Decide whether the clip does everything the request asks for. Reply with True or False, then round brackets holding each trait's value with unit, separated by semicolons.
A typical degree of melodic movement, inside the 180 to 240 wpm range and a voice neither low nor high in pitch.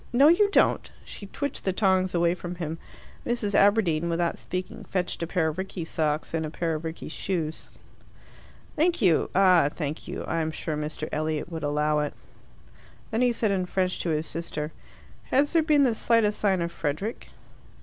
True (4.4 semitones; 185 wpm; 175 Hz)